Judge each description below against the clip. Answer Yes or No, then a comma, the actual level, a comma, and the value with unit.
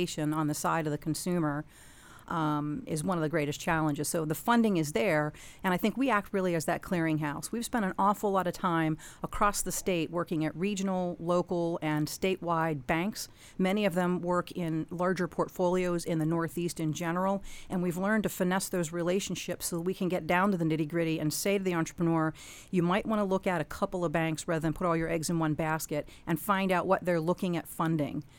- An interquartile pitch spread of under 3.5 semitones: Yes, average, 2.8 semitones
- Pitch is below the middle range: No, medium, 175 Hz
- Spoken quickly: Yes, fast, 220 wpm